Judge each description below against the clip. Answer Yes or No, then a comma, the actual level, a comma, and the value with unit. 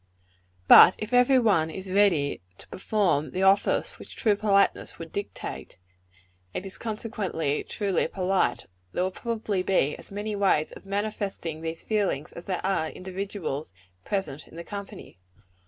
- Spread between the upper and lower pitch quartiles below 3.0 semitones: No, average, 3.8 semitones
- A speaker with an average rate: Yes, average, 150 wpm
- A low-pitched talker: No, high, 195 Hz